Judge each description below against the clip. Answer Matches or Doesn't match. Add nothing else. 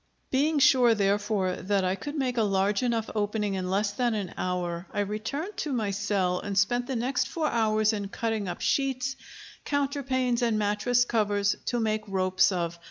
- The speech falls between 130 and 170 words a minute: Doesn't match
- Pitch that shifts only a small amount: Doesn't match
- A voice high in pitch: Matches